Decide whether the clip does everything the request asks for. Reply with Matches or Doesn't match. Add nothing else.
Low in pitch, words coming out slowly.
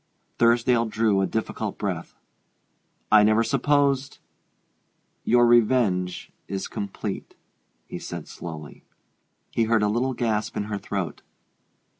Matches